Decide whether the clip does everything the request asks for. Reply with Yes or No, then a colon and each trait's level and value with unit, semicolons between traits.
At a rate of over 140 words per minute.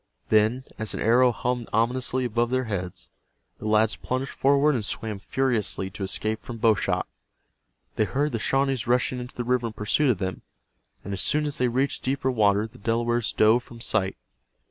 Yes: average, 190 wpm